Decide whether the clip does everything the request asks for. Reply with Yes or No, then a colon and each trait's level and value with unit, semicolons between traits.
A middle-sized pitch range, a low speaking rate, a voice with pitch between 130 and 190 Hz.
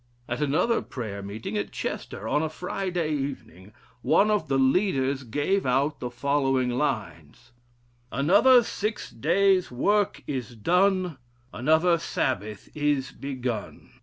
No: wide, 6.5 semitones; slow, 125 wpm; medium, 140 Hz